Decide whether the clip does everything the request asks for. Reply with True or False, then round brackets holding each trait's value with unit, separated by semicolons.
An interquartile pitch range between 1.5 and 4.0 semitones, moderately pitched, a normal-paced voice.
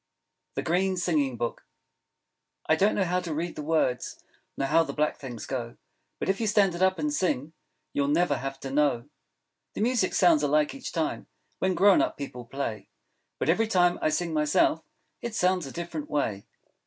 False (4.7 semitones; 160 Hz; 190 wpm)